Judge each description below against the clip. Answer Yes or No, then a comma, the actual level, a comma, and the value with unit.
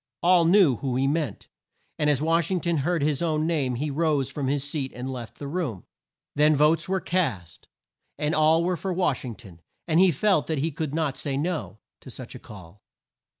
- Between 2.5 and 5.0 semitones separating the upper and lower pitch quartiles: Yes, average, 3.8 semitones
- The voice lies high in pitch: No, medium, 150 Hz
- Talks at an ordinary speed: No, fast, 210 wpm